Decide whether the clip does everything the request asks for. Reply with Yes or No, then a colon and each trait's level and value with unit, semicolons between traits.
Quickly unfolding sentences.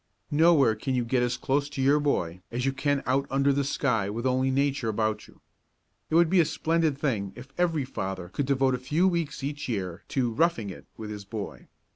Yes: fast, 215 wpm